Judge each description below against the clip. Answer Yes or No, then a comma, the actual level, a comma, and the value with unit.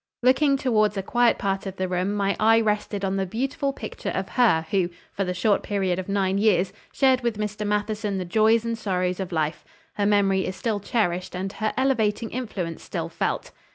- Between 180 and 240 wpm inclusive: Yes, average, 200 wpm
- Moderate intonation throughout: Yes, average, 3.0 semitones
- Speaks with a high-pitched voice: Yes, high, 205 Hz